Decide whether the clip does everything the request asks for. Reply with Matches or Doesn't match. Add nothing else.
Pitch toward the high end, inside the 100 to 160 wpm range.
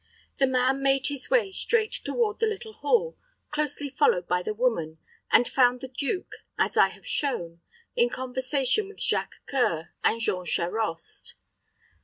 Matches